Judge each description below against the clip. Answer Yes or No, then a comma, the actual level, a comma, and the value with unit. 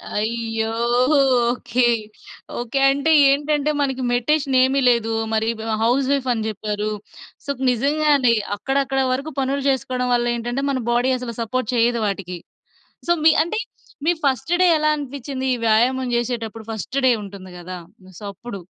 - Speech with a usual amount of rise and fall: Yes, average, 3.5 semitones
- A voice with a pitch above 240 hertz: Yes, very high, 250 Hz